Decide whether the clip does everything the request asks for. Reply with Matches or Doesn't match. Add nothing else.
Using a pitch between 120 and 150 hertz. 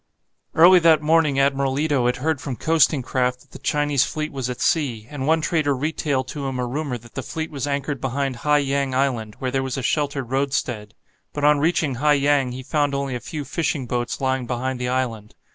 Matches